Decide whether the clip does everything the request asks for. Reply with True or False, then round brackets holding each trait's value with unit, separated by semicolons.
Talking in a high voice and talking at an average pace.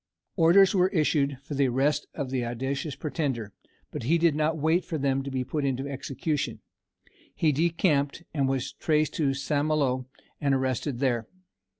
False (140 Hz; 170 wpm)